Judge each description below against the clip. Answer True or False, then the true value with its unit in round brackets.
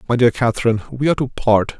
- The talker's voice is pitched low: True (120 Hz)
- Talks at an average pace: False (235 wpm)